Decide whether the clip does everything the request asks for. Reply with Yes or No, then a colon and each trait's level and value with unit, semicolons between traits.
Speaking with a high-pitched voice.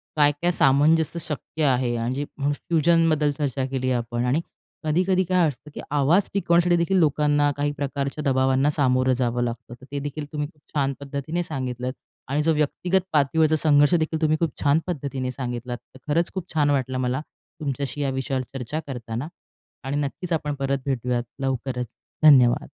No: medium, 145 Hz